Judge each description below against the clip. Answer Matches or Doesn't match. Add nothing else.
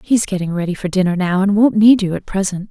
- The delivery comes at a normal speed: Doesn't match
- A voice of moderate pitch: Doesn't match